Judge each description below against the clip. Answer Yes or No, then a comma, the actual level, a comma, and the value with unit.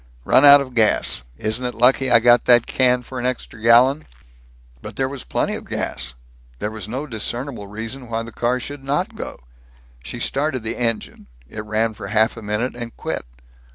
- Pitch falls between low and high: No, low, 120 Hz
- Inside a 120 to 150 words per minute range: No, average, 190 wpm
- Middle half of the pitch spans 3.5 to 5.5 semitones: No, average, 2.8 semitones